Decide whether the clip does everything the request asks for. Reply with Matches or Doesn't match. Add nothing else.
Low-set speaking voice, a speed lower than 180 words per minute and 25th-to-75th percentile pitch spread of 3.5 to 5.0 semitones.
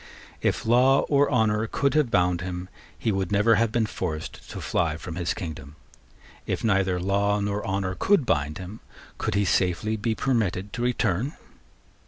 Matches